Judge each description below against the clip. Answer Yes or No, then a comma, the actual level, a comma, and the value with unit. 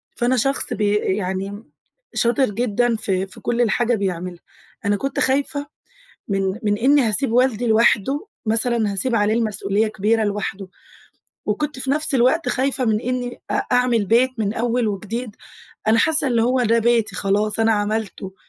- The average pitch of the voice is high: Yes, high, 225 Hz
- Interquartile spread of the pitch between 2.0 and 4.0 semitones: Yes, average, 3.2 semitones